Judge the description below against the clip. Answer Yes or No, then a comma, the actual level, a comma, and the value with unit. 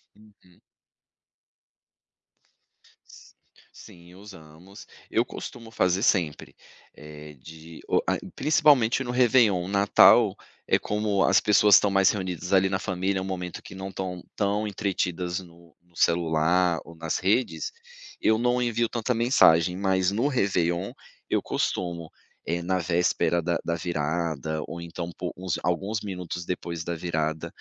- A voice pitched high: No, very low, 90 Hz